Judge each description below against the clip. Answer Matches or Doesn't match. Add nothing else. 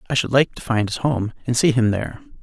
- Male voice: Matches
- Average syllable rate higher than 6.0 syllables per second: Matches